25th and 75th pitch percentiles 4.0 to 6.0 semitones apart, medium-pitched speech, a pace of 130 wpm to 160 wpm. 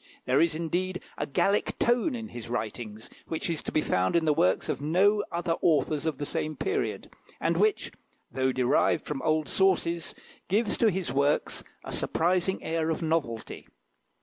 No: average, 5.1 semitones; medium, 160 Hz; average, 175 wpm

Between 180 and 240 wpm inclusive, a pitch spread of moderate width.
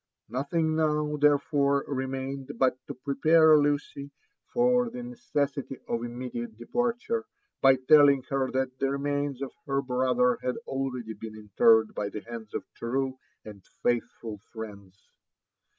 No: slow, 135 wpm; average, 3.3 semitones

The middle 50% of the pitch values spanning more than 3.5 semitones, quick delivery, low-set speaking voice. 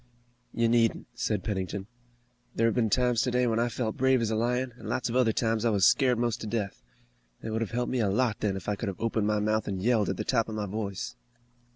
No: narrow, 2.5 semitones; fast, 255 wpm; low, 115 Hz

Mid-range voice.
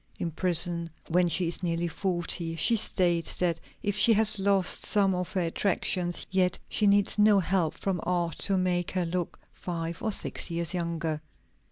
Yes: medium, 180 Hz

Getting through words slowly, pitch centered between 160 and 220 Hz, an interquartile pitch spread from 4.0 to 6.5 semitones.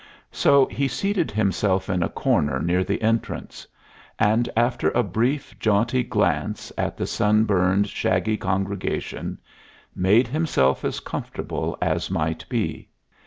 No: slow, 125 wpm; low, 105 Hz; average, 4.4 semitones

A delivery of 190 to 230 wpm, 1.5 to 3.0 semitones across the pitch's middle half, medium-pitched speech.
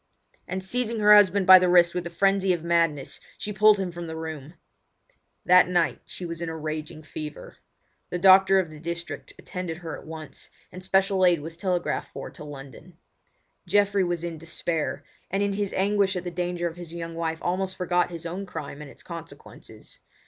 Yes: average, 195 wpm; narrow, 2.6 semitones; medium, 175 Hz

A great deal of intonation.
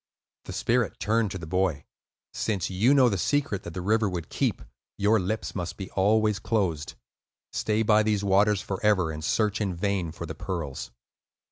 No: average, 3.3 semitones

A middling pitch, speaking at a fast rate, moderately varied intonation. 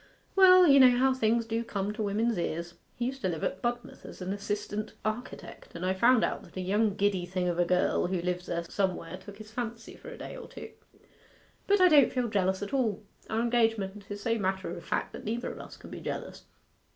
No: high, 215 Hz; fast, 230 wpm; average, 4.2 semitones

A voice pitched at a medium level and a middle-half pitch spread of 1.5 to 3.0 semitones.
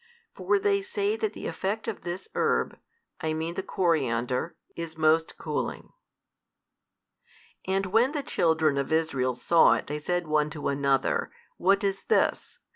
No: medium, 165 Hz; average, 4.7 semitones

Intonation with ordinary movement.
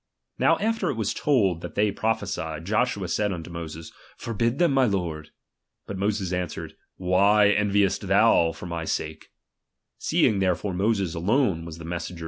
Yes: average, 4.0 semitones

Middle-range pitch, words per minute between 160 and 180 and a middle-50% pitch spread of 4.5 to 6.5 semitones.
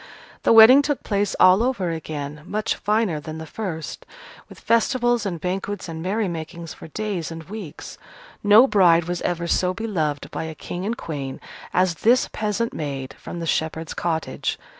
Yes: medium, 180 Hz; average, 165 wpm; average, 5.0 semitones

